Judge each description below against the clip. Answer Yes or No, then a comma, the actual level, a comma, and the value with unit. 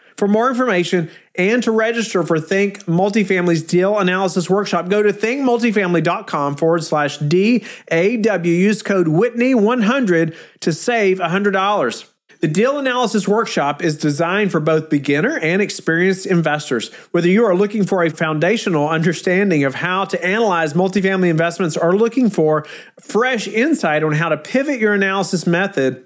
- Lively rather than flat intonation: No, average, 4.2 semitones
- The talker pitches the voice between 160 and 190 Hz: Yes, medium, 185 Hz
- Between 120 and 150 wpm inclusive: Yes, average, 145 wpm